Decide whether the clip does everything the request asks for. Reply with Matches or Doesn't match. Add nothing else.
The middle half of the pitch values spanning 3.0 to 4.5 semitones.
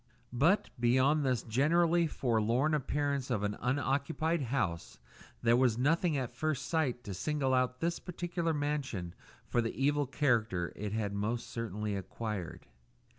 Doesn't match